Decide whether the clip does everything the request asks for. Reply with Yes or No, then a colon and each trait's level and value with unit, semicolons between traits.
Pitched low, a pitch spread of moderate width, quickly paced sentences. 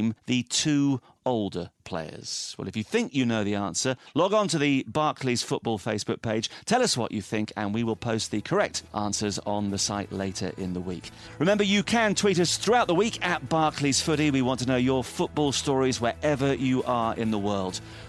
Yes: low, 115 Hz; average, 4.9 semitones; fast, 210 wpm